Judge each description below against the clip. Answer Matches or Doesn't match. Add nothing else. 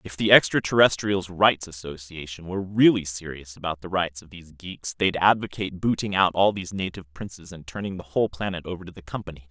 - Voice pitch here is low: Matches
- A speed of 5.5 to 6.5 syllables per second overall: Matches